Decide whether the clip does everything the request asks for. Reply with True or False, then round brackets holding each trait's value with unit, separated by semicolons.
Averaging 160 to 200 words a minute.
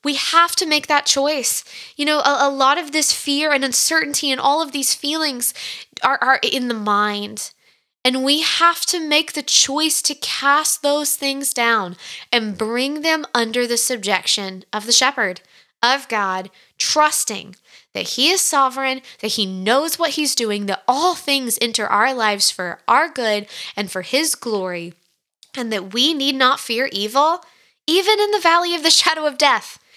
True (180 wpm)